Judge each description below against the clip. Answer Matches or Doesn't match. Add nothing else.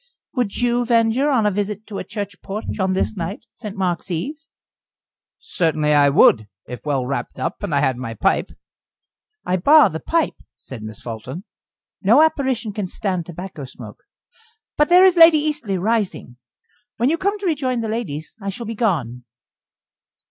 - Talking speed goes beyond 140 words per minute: Matches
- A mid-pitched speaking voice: Doesn't match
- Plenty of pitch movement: Matches